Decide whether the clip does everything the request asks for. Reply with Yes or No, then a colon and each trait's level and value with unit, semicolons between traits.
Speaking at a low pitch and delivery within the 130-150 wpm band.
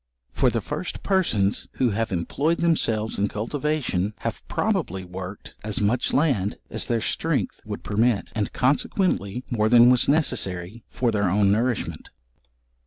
Yes: low, 110 Hz; average, 145 wpm